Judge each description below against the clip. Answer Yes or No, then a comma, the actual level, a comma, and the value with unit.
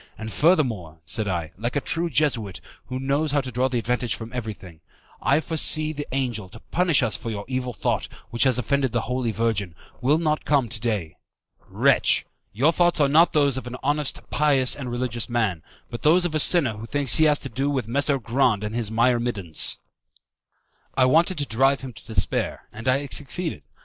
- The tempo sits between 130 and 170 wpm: No, average, 200 wpm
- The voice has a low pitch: Yes, low, 130 Hz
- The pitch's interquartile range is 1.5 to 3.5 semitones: No, average, 4.3 semitones